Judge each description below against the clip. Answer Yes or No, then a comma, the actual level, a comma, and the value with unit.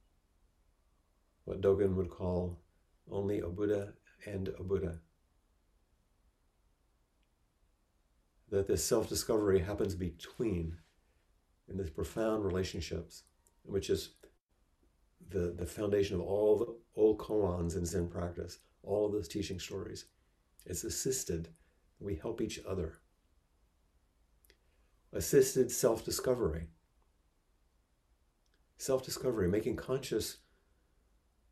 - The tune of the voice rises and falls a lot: No, average, 4.5 semitones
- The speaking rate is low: Yes, slow, 90 wpm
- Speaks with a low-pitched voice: Yes, very low, 85 Hz